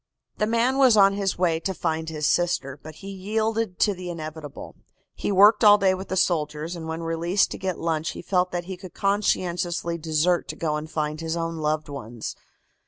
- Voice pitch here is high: No, medium, 175 Hz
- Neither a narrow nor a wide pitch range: Yes, average, 3.5 semitones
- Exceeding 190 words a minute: Yes, fast, 205 wpm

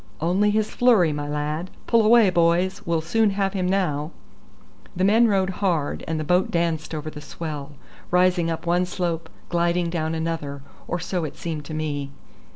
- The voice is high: No, medium, 170 Hz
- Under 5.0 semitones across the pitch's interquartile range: Yes, average, 3.2 semitones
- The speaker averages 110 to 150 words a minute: No, average, 175 wpm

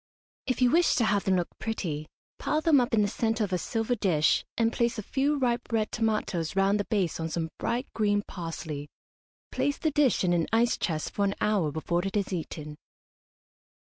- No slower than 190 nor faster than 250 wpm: Yes, fast, 205 wpm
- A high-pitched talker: Yes, high, 205 Hz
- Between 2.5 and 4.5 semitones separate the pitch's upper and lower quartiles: No, average, 5.3 semitones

